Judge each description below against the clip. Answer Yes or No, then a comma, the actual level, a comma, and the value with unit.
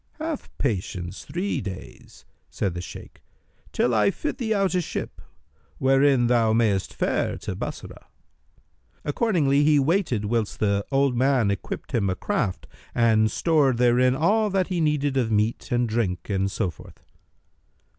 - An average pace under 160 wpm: Yes, average, 150 wpm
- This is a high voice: No, low, 125 Hz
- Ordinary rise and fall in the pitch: No, wide, 6.0 semitones